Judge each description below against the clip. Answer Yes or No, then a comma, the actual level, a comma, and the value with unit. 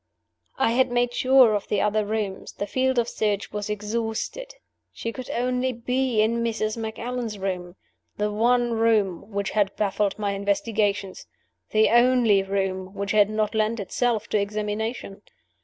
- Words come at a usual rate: Yes, average, 155 wpm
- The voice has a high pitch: Yes, high, 215 Hz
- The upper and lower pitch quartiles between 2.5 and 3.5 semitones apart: Yes, average, 2.8 semitones